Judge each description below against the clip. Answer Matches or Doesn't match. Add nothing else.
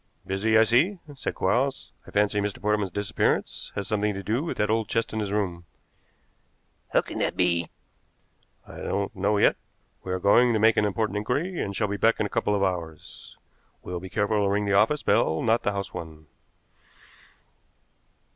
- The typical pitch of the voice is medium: Doesn't match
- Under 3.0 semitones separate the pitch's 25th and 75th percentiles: Matches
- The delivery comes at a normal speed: Matches